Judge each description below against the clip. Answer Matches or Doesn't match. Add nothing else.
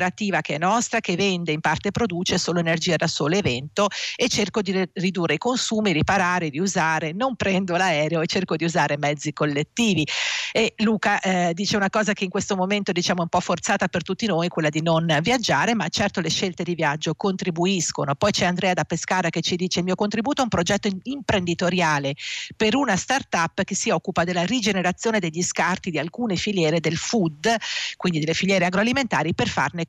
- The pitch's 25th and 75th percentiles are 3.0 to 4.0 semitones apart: Matches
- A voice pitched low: Doesn't match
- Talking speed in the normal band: Doesn't match